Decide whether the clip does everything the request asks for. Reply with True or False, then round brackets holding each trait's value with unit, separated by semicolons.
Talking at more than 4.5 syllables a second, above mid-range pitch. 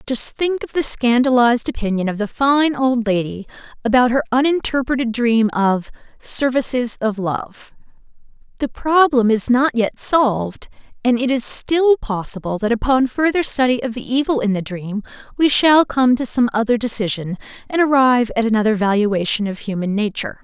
True (5.0 syllables/s; 240 Hz)